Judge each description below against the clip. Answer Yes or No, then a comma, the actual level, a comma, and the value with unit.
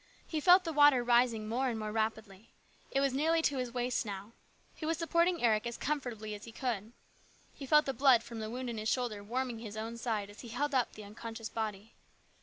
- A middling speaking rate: No, fast, 220 wpm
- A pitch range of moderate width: Yes, average, 3.8 semitones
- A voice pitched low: No, high, 235 Hz